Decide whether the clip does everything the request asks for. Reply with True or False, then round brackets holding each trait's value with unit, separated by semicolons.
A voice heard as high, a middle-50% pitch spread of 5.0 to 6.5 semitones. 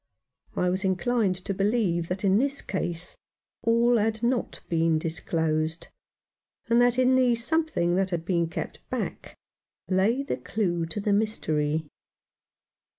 True (195 Hz; 5.6 semitones)